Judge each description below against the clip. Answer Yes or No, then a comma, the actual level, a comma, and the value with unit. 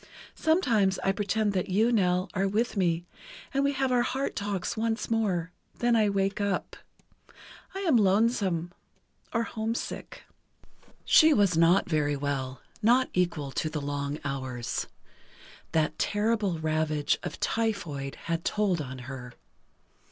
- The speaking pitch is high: Yes, high, 195 Hz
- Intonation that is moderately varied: No, wide, 6.1 semitones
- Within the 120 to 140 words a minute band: Yes, slow, 135 wpm